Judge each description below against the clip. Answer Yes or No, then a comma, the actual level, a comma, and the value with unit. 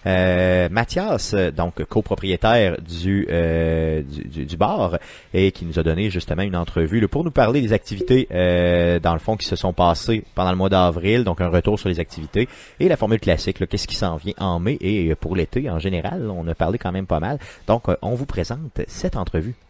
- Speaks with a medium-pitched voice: No, very low, 90 Hz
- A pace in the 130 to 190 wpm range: No, average, 215 wpm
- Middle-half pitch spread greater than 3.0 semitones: Yes, average, 3.6 semitones